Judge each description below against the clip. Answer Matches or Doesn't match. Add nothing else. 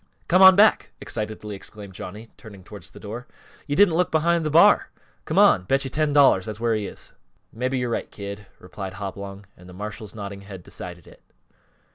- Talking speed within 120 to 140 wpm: Doesn't match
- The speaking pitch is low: Matches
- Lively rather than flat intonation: Matches